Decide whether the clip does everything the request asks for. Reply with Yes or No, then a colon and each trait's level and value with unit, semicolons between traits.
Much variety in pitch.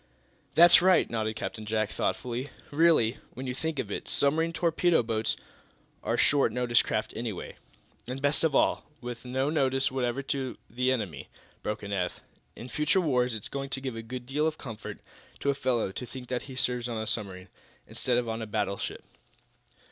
No: average, 3.8 semitones